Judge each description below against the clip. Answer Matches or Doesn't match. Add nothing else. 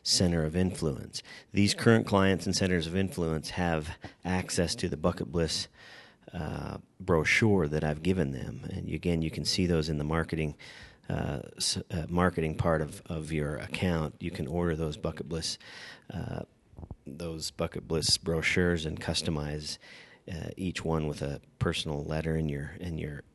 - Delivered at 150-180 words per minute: Matches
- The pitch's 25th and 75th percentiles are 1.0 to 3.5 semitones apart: Matches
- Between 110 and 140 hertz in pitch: Doesn't match